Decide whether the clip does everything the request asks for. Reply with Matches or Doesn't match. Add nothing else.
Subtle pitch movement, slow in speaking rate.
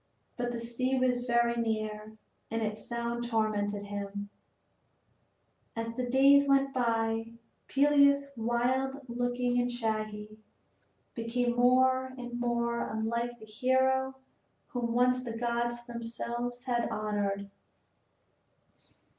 Matches